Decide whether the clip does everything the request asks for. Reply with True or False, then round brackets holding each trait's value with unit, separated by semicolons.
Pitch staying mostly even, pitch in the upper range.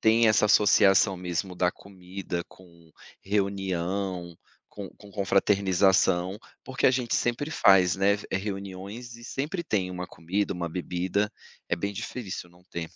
False (2.3 semitones; 95 Hz)